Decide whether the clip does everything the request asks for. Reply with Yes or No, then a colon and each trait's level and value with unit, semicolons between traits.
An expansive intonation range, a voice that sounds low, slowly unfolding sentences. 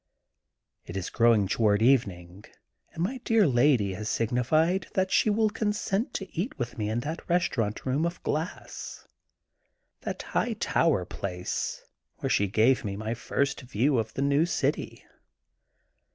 No: wide, 8.0 semitones; low, 130 Hz; average, 150 wpm